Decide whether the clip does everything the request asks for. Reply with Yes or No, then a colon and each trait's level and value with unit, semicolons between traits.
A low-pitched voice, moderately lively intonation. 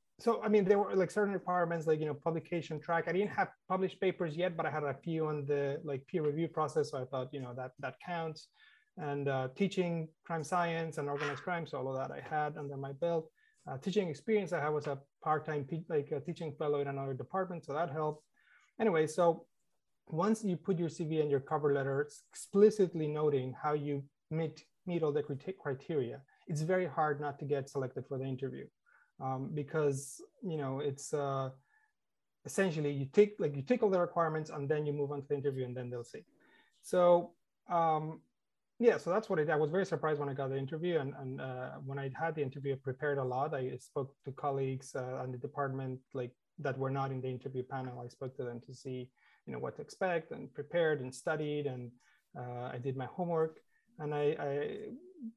No: medium, 150 Hz; average, 3.9 semitones